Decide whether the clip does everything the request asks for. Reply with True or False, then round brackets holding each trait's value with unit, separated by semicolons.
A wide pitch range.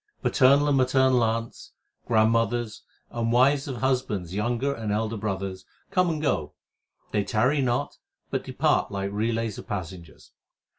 False (3.9 semitones)